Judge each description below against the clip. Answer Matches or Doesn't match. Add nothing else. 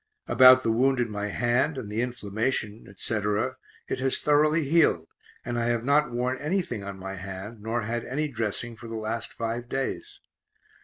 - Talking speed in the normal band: Matches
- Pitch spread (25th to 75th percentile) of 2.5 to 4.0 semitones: Matches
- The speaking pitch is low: Matches